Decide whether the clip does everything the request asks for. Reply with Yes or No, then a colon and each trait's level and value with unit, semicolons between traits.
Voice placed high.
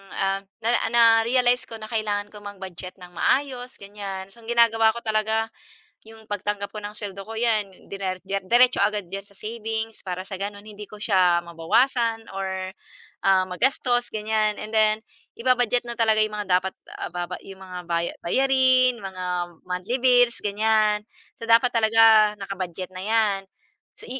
Yes: high, 215 Hz